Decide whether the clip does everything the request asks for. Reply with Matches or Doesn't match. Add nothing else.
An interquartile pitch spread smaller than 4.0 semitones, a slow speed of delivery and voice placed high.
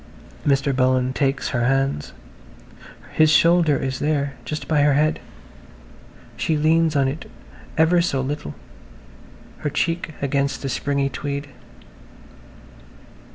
Doesn't match